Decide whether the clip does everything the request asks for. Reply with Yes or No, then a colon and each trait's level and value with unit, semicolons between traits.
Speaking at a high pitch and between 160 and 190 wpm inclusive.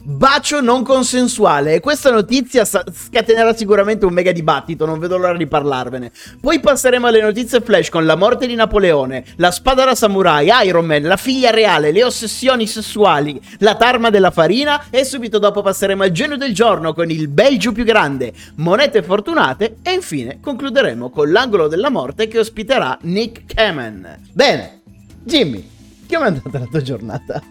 Yes: high, 210 Hz; average, 165 wpm